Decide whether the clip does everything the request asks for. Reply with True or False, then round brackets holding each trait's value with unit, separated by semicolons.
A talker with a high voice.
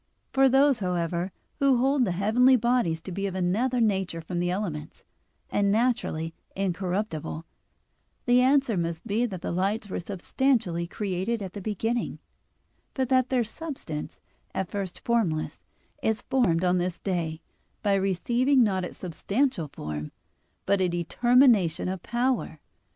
True (200 Hz)